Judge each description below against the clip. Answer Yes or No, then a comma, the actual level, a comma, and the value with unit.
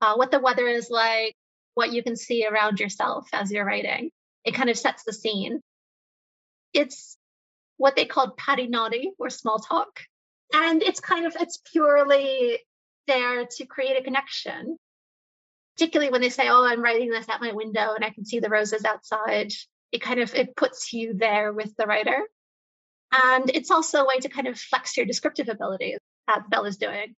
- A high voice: Yes, high, 245 Hz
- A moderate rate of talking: Yes, average, 185 wpm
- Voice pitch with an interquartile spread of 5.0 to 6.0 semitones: No, average, 4.1 semitones